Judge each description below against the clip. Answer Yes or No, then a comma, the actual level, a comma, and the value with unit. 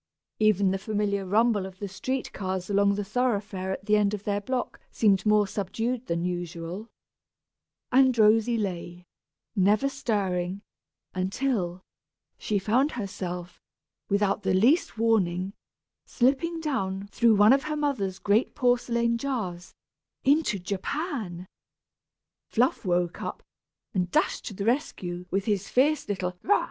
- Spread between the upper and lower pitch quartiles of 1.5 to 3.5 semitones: No, average, 4.3 semitones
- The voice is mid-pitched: No, high, 205 Hz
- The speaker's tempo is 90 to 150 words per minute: Yes, slow, 135 wpm